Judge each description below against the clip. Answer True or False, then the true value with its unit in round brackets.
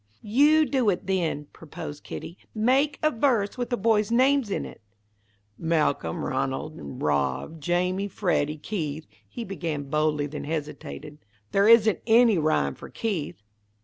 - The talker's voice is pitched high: False (180 Hz)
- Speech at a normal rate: True (145 wpm)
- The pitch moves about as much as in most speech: False (7.2 semitones)